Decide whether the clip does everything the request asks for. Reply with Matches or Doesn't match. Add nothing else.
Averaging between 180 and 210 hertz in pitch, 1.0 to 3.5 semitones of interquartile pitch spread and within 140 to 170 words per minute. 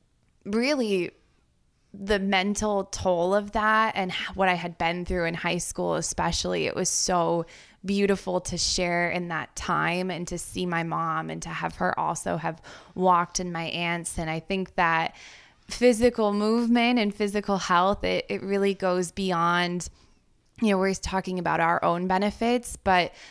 Matches